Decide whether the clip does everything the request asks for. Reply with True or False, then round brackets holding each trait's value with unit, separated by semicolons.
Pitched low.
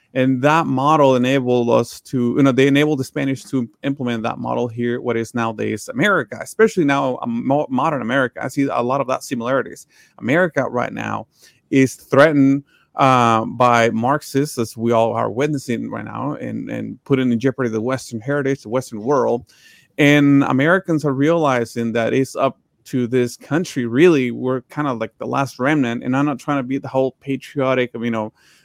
True (130 Hz)